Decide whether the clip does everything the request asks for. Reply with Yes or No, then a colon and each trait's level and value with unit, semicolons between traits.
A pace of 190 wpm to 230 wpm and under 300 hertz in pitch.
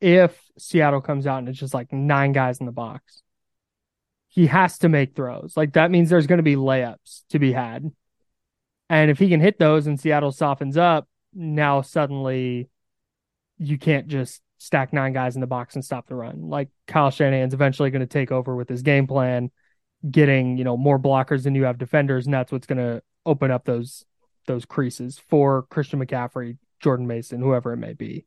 Yes: average, 200 wpm; low, 135 Hz